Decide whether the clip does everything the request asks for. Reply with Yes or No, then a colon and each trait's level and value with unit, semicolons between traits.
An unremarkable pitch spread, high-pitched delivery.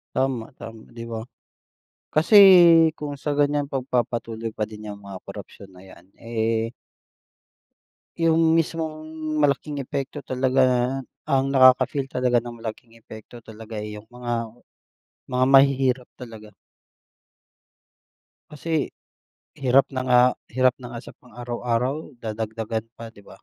No: average, 3.3 semitones; low, 125 Hz